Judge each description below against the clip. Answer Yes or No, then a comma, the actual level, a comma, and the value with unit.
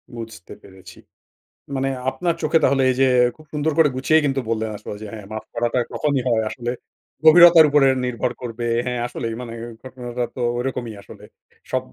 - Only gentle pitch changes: No, average, 3.7 semitones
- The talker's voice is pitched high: No, low, 125 Hz